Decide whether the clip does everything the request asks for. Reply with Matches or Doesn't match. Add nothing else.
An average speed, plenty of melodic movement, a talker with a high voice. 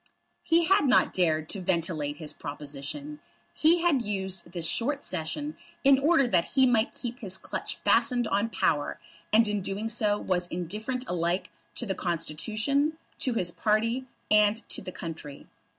Matches